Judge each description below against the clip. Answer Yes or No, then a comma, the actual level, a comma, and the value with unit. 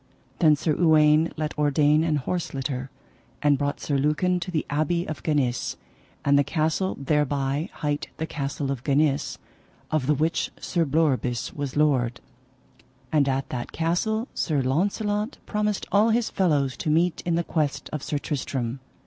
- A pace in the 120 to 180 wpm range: Yes, average, 160 wpm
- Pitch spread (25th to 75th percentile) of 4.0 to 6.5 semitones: No, average, 3.1 semitones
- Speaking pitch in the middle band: Yes, medium, 150 Hz